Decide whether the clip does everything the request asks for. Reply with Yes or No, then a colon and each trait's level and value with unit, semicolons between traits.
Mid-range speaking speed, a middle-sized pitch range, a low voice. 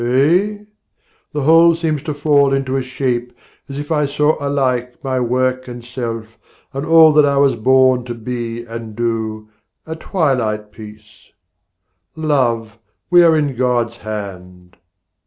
Yes: average, 145 wpm; average, 4.1 semitones; low, 130 Hz